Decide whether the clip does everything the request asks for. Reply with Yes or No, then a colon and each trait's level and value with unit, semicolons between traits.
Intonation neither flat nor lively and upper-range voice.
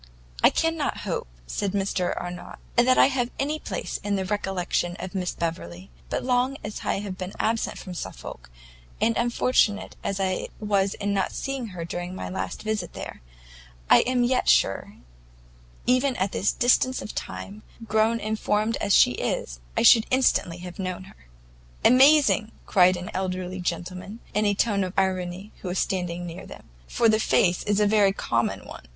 Yes: average, 3.9 semitones; high, 200 Hz